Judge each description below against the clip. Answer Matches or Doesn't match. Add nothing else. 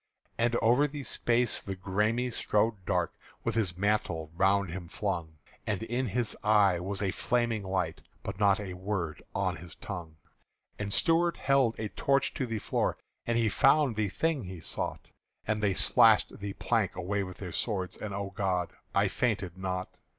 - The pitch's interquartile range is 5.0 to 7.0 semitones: Doesn't match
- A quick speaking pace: Doesn't match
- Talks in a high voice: Doesn't match